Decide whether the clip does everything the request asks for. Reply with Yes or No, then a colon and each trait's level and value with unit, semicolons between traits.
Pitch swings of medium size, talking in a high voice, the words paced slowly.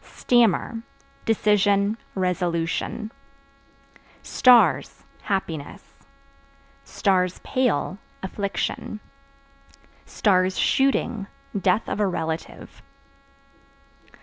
Yes: average, 3.4 semitones; high, 195 Hz; slow, 45 wpm